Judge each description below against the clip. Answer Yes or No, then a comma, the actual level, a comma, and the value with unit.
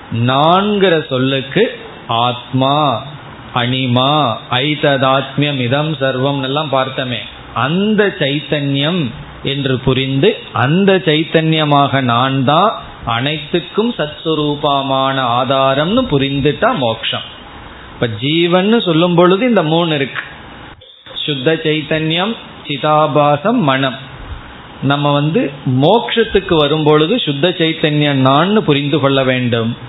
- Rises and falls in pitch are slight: No, average, 3.3 semitones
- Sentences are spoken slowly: Yes, slow, 70 wpm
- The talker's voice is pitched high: No, medium, 145 Hz